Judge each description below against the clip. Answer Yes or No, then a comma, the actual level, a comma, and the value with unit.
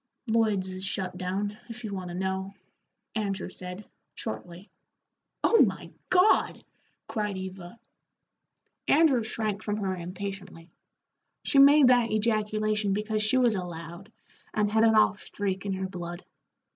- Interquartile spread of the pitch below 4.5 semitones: Yes, average, 2.7 semitones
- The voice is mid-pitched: No, high, 205 Hz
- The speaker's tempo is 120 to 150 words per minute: Yes, average, 140 wpm